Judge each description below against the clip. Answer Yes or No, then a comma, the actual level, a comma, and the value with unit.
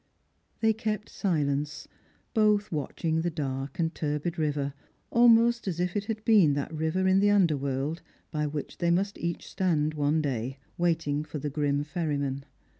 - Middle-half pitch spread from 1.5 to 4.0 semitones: No, average, 4.5 semitones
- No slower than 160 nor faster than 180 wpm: Yes, average, 165 wpm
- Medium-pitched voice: Yes, medium, 160 Hz